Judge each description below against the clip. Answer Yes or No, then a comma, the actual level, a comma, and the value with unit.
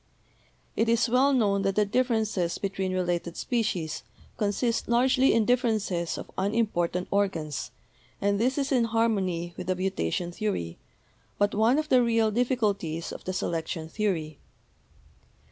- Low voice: No, high, 205 Hz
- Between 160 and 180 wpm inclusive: No, average, 145 wpm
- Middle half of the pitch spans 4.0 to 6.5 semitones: Yes, average, 4.7 semitones